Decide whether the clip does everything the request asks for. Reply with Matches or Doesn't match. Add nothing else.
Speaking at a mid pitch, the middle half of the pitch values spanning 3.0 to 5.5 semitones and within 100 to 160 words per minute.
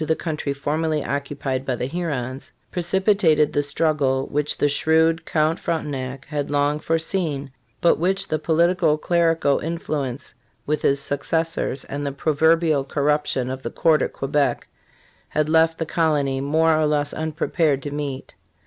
Doesn't match